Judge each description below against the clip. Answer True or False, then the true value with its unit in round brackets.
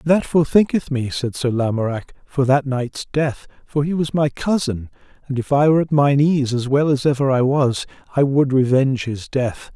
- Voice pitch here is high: False (135 Hz)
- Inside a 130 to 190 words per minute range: False (205 wpm)